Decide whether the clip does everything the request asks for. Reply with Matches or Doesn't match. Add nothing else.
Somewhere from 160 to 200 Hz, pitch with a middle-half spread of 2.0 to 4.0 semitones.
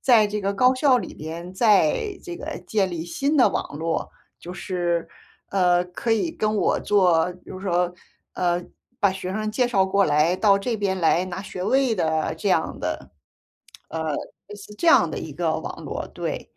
Matches